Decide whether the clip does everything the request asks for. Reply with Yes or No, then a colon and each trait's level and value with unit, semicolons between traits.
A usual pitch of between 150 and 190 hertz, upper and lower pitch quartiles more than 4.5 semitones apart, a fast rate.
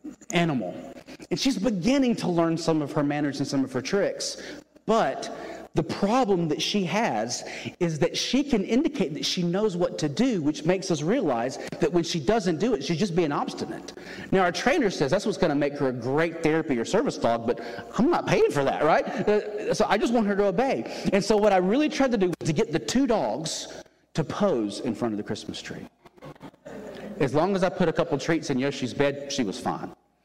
Yes: medium, 185 Hz; wide, 5.5 semitones; fast, 220 wpm